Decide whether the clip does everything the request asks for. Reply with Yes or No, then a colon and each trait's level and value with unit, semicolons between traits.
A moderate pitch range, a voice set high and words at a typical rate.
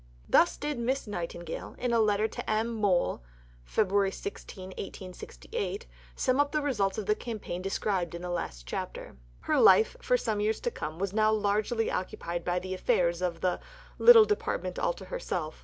Yes: average, 4.9 semitones; high, 205 Hz; average, 175 wpm